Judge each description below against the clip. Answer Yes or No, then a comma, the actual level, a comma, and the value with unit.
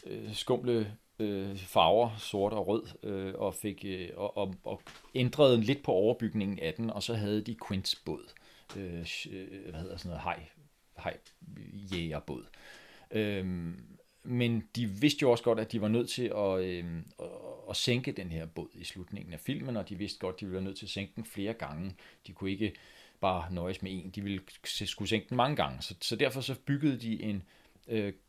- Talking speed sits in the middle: Yes, average, 200 wpm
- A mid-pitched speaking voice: No, low, 100 Hz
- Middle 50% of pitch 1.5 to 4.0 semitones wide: Yes, average, 3.3 semitones